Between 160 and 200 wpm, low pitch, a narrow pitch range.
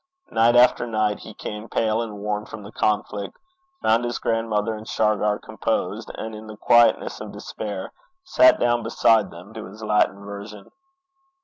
Yes: average, 165 wpm; low, 110 Hz; narrow, 1.5 semitones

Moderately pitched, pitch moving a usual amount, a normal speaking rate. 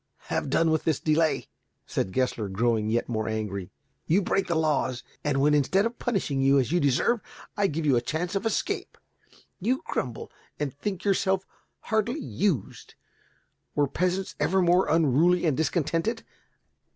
No: medium, 160 Hz; wide, 6.3 semitones; average, 160 wpm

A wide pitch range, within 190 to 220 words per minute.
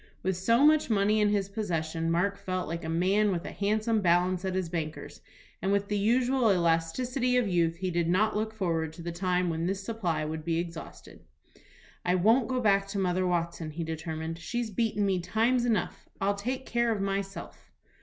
No: average, 4.2 semitones; average, 195 wpm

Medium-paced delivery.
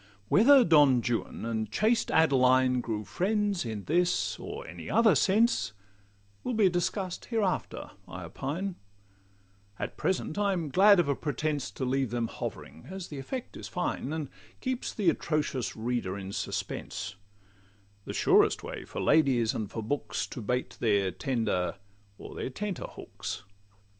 Yes: average, 150 wpm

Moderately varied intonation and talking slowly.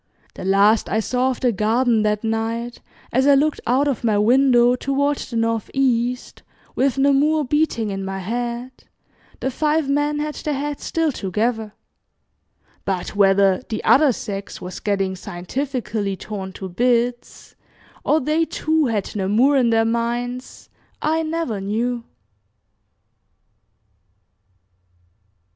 Yes: average, 4.5 semitones; slow, 130 wpm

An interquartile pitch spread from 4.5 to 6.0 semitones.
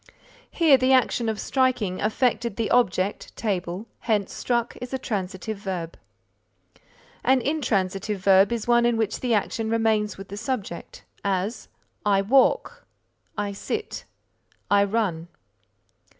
No: average, 3.6 semitones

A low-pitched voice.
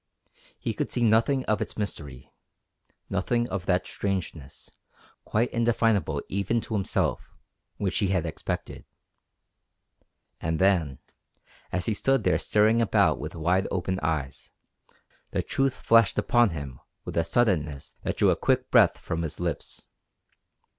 Yes: very low, 95 Hz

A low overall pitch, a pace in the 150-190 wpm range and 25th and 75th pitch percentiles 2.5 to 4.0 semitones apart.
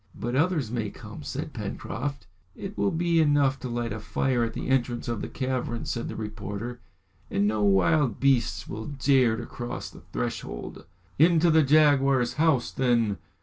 No: low, 125 Hz; average, 170 wpm; average, 4.4 semitones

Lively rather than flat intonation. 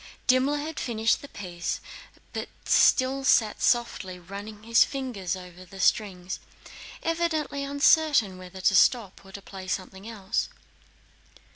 Yes: wide, 6.0 semitones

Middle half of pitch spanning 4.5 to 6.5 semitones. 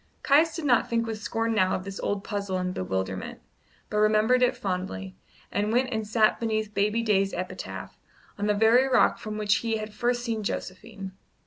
No: narrow, 2.6 semitones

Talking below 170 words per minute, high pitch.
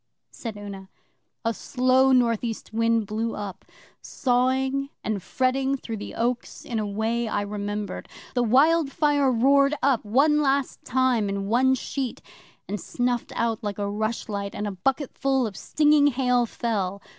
Yes: average, 150 wpm; high, 235 Hz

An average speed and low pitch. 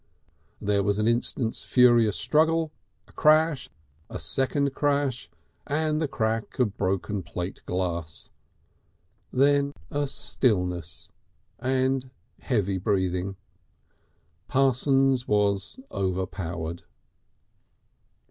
No: slow, 90 wpm; low, 115 Hz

